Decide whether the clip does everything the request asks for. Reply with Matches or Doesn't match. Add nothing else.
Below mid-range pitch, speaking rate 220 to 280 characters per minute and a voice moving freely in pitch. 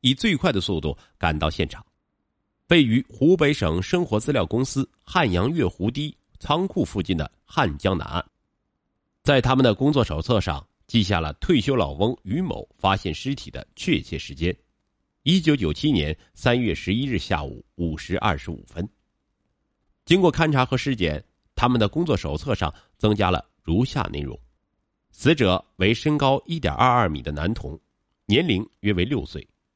Matches